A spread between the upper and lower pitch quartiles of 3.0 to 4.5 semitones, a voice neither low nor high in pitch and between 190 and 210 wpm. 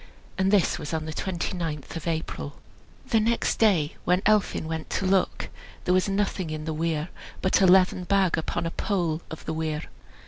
Yes: average, 3.3 semitones; medium, 175 Hz; average, 195 wpm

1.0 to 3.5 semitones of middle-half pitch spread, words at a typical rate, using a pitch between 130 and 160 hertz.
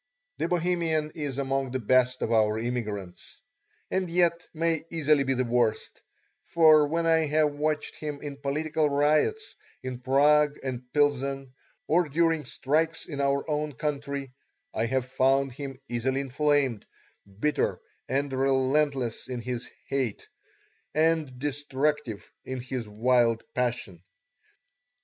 No: average, 3.1 semitones; slow, 130 wpm; medium, 140 Hz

